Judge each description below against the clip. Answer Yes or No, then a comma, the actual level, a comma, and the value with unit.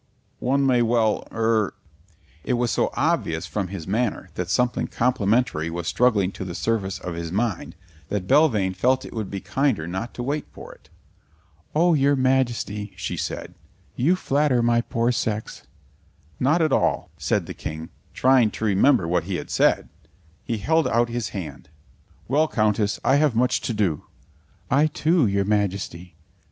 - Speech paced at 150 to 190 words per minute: Yes, average, 165 wpm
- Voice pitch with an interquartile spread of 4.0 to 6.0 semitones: Yes, average, 5.1 semitones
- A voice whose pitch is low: Yes, low, 115 Hz